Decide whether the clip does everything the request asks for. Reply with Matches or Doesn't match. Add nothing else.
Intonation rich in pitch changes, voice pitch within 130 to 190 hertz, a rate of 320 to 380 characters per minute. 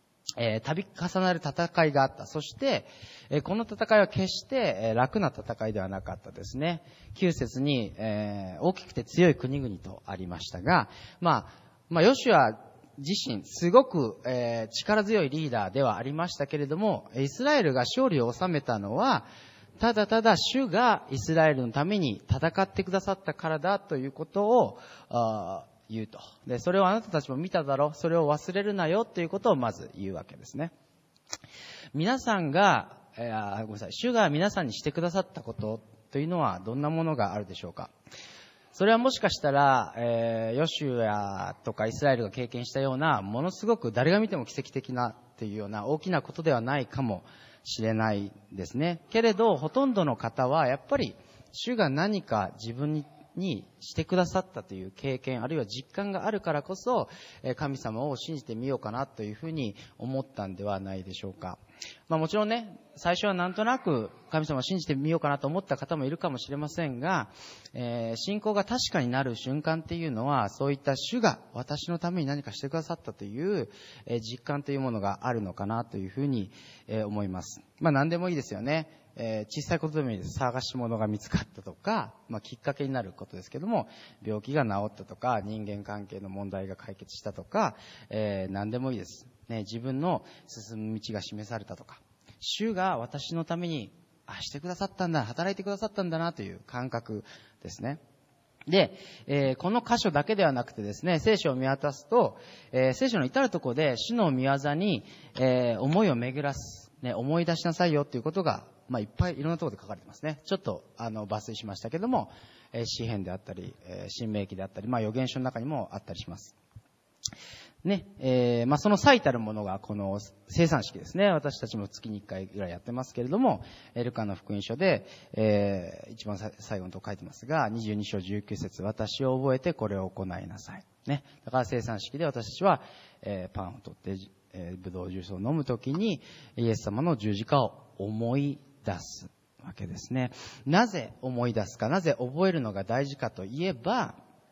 Matches